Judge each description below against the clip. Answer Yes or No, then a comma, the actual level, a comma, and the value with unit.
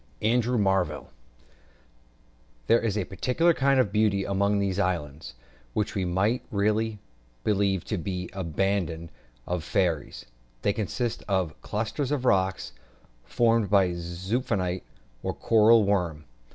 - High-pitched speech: No, low, 100 Hz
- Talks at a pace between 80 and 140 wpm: Yes, slow, 135 wpm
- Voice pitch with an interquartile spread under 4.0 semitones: Yes, average, 3.6 semitones